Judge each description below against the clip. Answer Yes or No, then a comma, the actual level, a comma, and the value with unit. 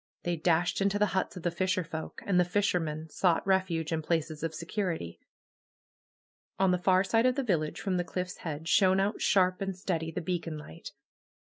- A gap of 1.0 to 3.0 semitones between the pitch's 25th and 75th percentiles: Yes, average, 2.7 semitones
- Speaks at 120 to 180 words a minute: No, average, 190 wpm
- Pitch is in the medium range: Yes, medium, 180 Hz